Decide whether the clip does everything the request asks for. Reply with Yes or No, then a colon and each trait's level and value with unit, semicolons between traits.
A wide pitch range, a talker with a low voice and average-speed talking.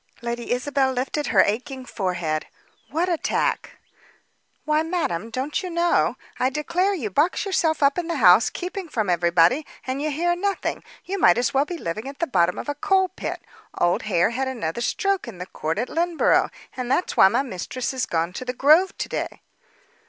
No: wide, 7.6 semitones; very high, 265 Hz; average, 190 wpm